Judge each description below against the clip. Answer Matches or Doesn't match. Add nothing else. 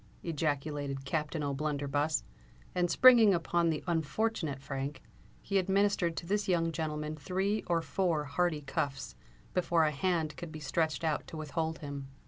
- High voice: Doesn't match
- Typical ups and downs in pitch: Matches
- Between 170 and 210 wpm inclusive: Doesn't match